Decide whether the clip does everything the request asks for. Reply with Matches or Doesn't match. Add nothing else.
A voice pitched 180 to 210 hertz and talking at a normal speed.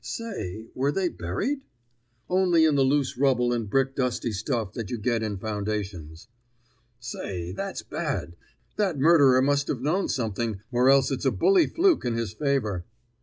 Doesn't match